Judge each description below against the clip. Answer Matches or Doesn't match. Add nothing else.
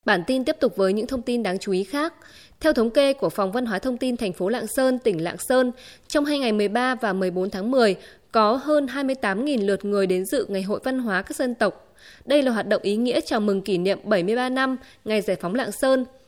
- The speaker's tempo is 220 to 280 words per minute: Matches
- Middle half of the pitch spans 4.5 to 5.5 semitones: Matches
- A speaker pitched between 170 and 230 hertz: Doesn't match